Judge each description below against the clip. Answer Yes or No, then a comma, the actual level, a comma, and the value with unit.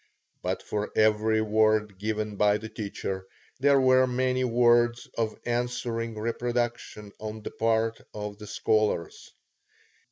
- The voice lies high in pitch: No, low, 110 Hz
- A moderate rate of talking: No, slow, 125 wpm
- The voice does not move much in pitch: Yes, narrow, 2.0 semitones